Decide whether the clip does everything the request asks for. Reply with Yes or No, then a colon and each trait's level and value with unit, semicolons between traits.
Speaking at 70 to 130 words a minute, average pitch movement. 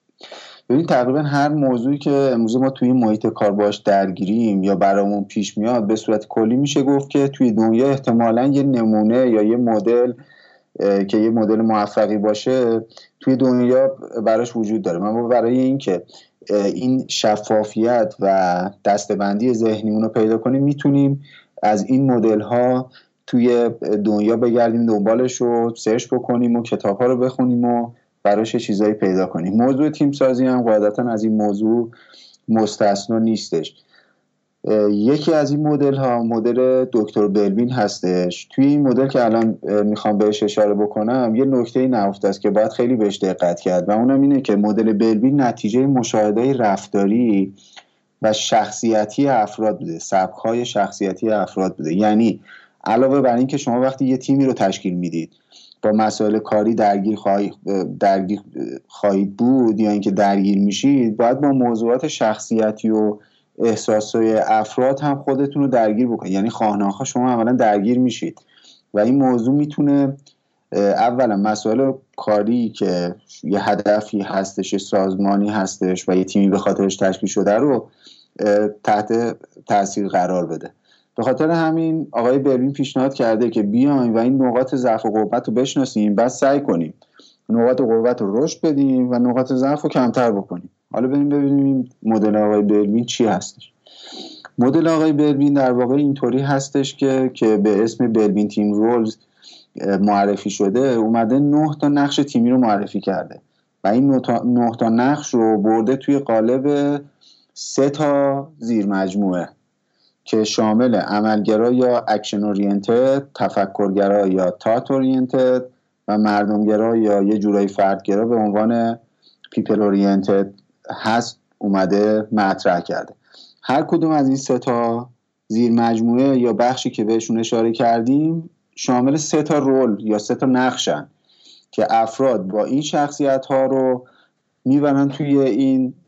No: average, 145 wpm; average, 3.8 semitones